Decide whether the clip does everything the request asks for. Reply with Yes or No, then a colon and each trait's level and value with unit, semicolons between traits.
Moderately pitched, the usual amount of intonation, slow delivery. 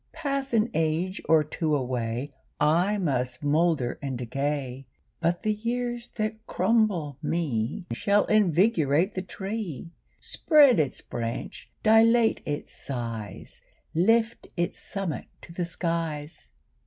No: medium, 170 Hz; wide, 7.1 semitones; slow, 115 wpm